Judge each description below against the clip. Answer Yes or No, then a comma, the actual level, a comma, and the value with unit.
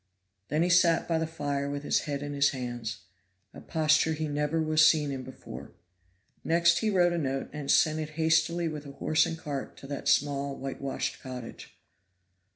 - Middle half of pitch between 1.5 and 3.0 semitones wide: Yes, narrow, 2.6 semitones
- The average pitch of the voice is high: No, medium, 150 Hz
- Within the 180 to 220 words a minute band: Yes, average, 185 wpm